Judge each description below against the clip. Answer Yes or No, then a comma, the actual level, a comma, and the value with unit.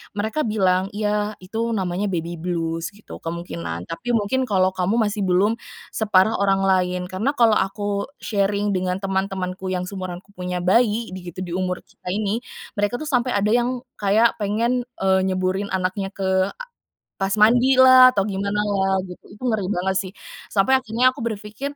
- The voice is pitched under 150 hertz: No, high, 200 Hz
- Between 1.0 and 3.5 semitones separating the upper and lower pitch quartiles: Yes, average, 2.9 semitones